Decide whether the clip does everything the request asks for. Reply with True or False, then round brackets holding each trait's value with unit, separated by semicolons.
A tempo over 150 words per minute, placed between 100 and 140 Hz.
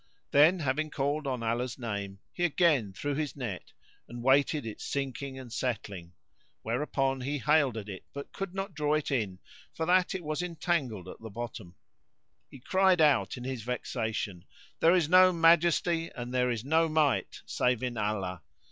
True (175 wpm; 135 Hz)